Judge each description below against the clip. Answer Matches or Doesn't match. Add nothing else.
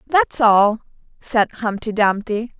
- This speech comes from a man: Doesn't match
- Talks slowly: Matches